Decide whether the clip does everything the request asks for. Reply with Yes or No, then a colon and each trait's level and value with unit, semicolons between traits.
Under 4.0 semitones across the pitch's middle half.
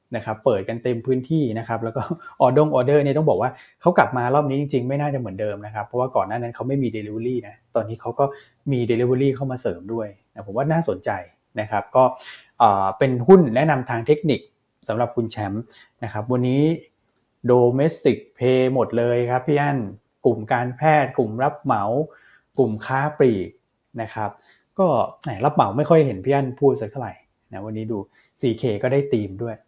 Yes: average, 3.5 semitones